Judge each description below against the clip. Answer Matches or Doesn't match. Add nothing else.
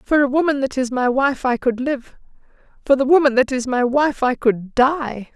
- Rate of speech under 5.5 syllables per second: Matches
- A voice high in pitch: Matches